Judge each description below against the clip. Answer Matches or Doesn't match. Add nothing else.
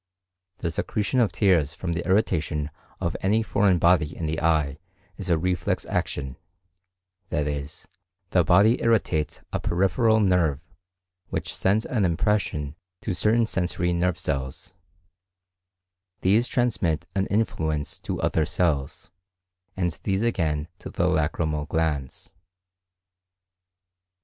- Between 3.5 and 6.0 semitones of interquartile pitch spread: Matches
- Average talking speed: Doesn't match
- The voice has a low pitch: Matches